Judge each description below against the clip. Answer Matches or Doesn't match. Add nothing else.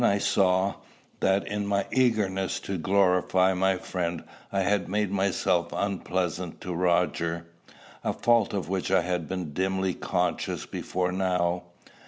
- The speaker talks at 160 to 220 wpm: Doesn't match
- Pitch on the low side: Matches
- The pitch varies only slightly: Matches